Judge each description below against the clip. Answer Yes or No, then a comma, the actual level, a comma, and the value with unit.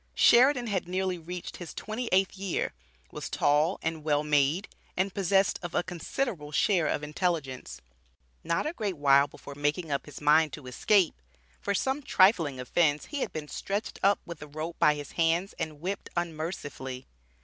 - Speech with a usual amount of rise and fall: Yes, average, 4.6 semitones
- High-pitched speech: No, medium, 170 Hz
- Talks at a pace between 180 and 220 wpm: No, average, 170 wpm